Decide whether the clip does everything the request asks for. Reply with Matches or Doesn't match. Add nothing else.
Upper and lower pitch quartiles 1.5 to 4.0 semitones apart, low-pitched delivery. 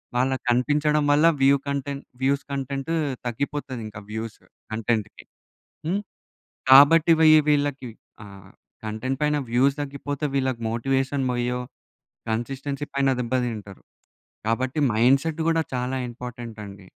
Matches